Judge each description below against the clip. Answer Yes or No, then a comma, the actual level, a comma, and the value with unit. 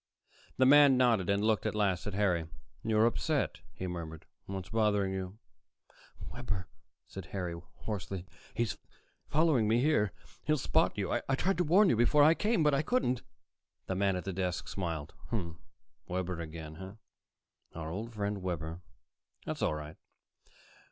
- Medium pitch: No, low, 100 Hz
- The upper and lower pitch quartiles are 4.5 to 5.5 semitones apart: Yes, average, 5.2 semitones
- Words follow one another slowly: No, average, 155 wpm